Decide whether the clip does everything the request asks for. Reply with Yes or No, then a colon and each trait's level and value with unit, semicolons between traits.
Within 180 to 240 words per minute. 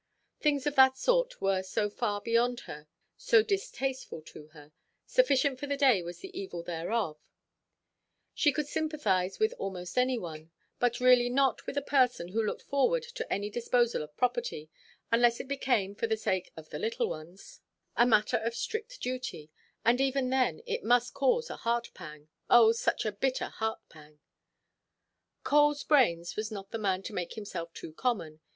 No: average, 170 wpm